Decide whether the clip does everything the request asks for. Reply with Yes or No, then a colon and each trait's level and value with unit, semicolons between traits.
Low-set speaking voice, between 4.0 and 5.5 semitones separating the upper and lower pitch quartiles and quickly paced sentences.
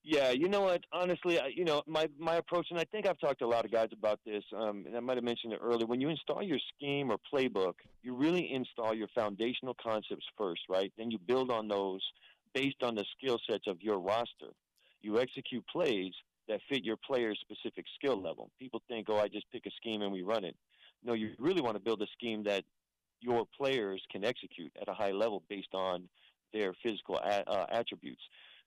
Yes: low, 115 Hz; average, 4.4 semitones; fast, 220 wpm